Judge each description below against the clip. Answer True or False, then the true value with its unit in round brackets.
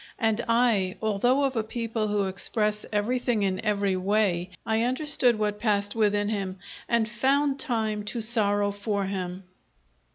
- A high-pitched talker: True (215 Hz)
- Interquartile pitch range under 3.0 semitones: True (2.6 semitones)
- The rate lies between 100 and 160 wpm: True (150 wpm)